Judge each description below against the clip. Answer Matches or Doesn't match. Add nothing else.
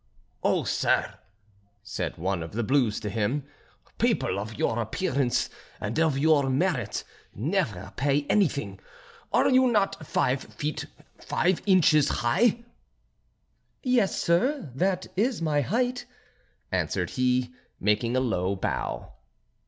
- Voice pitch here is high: Doesn't match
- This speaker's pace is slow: Matches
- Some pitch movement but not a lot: Doesn't match